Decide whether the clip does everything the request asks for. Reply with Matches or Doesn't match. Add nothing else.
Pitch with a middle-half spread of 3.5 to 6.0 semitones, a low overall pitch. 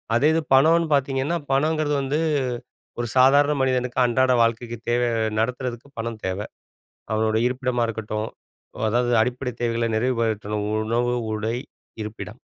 Doesn't match